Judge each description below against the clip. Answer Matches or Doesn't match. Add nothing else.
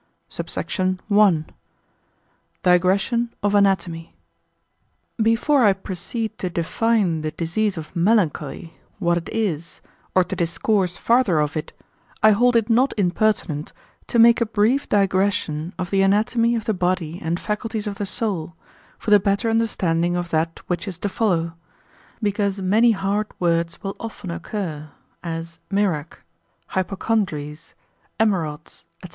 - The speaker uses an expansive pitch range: Doesn't match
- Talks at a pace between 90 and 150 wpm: Matches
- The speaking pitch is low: Doesn't match